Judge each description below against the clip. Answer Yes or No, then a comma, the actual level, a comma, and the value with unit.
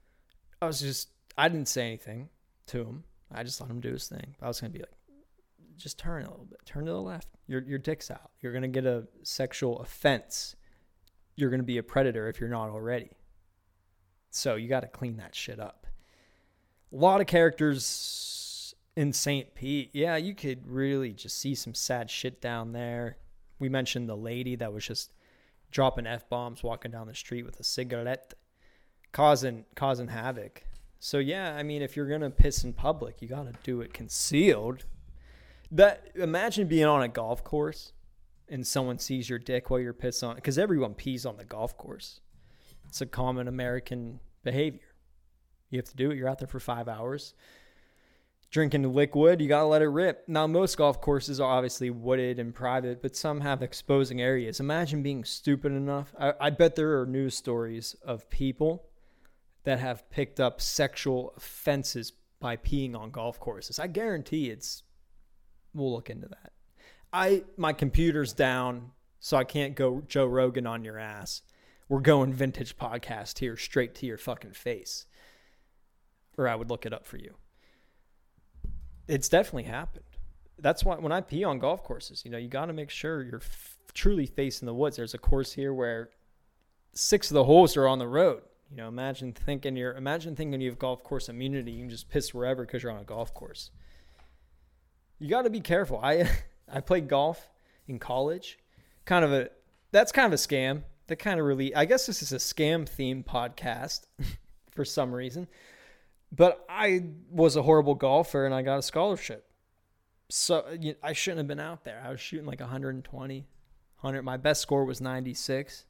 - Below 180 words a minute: No, average, 185 wpm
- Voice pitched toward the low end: Yes, low, 130 Hz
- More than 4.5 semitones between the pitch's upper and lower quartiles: No, average, 3.7 semitones